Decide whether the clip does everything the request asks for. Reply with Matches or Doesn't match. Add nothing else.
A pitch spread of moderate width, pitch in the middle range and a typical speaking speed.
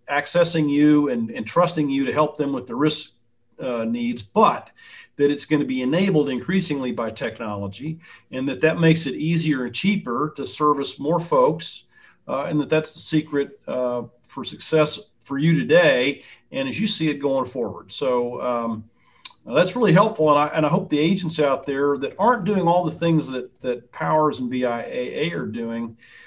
Matches